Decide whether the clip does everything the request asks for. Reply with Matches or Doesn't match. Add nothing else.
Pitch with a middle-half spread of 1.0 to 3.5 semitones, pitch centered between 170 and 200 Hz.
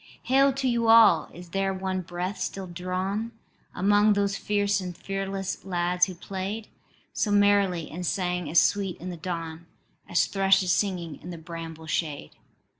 Matches